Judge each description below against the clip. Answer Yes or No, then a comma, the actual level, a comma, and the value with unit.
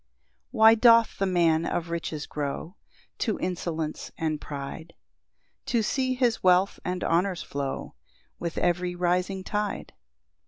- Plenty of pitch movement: No, average, 4.0 semitones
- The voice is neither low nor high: Yes, medium, 180 Hz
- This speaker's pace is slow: Yes, slow, 130 wpm